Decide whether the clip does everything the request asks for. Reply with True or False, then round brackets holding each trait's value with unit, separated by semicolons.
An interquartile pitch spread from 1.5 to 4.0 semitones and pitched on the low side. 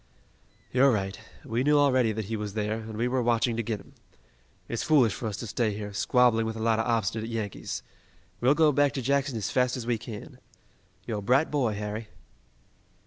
True (2.9 semitones; 115 Hz)